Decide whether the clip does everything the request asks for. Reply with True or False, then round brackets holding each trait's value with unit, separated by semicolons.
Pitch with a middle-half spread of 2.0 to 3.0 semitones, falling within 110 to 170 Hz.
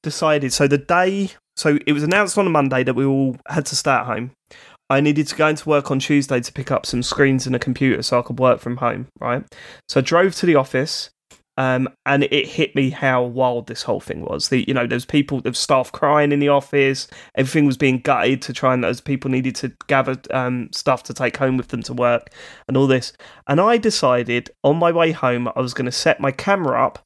True (2.6 semitones; 135 Hz)